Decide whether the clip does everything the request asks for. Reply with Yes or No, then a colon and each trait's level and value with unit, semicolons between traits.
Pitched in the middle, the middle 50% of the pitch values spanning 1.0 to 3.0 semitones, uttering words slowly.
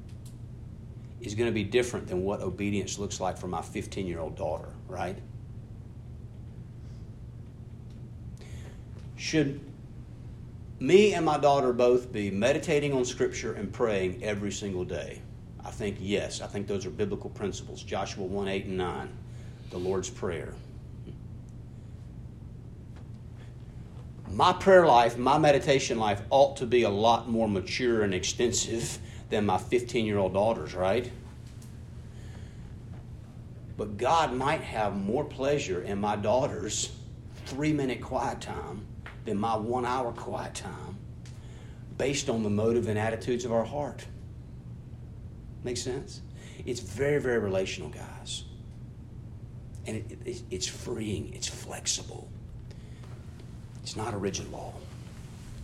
No: low, 115 Hz; narrow, 2.5 semitones; slow, 125 wpm